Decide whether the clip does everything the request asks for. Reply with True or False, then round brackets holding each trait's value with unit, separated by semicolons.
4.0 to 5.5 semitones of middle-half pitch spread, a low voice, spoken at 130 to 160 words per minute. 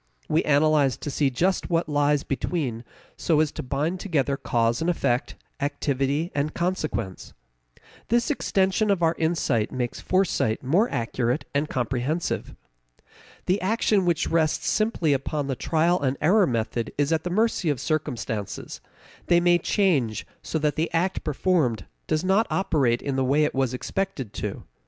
False (4.9 semitones; 150 Hz; 155 wpm)